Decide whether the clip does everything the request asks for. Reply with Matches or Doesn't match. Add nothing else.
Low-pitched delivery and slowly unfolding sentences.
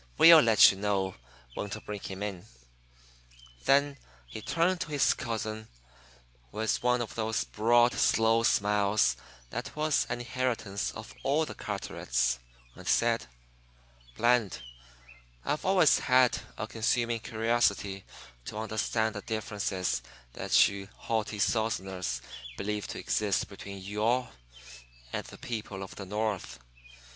Matches